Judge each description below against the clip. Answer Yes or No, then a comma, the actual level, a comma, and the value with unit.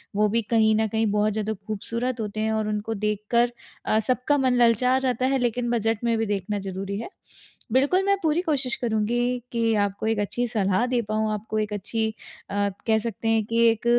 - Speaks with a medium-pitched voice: No, high, 225 Hz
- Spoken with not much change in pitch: Yes, narrow, 2.3 semitones